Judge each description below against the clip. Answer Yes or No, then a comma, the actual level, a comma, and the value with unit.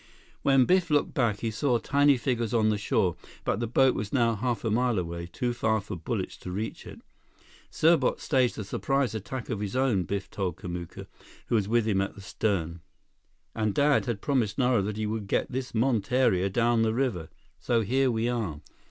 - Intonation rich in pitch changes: No, average, 4.1 semitones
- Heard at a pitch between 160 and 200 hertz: No, low, 115 Hz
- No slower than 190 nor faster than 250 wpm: Yes, average, 200 wpm